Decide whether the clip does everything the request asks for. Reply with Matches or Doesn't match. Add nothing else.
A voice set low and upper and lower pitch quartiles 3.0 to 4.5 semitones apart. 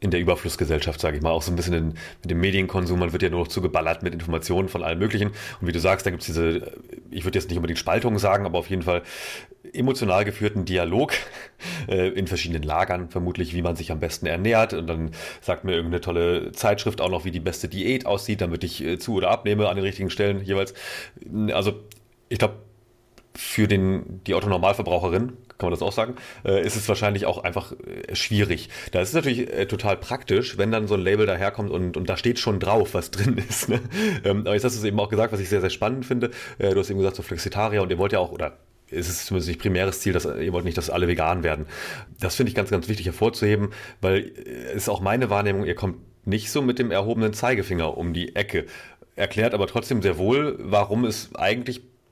Matches